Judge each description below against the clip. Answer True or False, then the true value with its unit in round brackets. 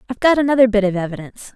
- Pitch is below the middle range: False (225 Hz)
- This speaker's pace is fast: True (230 wpm)